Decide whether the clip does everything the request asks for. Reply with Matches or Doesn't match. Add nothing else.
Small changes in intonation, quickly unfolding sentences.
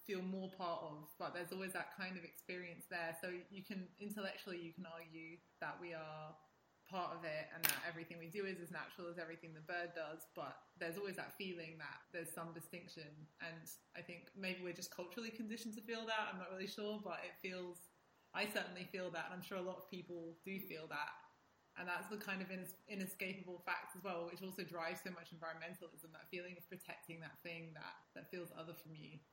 Matches